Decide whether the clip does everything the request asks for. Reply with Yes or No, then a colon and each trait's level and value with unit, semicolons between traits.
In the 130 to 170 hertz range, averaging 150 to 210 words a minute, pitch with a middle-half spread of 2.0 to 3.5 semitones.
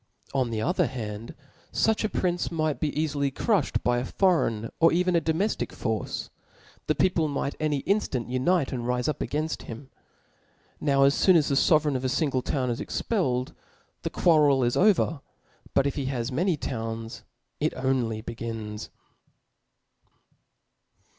No: medium, 140 Hz; average, 155 wpm; average, 4.8 semitones